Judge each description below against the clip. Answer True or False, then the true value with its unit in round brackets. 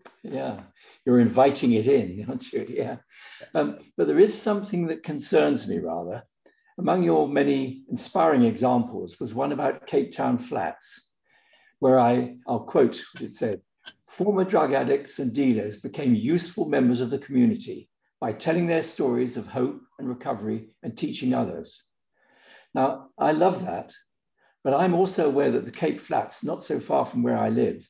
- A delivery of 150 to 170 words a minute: True (160 wpm)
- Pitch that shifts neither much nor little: False (8.3 semitones)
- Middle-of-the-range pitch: True (150 Hz)